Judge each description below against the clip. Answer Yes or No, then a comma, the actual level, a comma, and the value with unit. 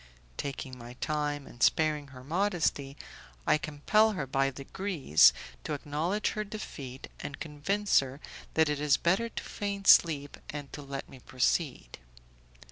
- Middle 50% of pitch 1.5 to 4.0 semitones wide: No, average, 4.4 semitones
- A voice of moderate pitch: Yes, medium, 150 Hz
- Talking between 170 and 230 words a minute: No, average, 145 wpm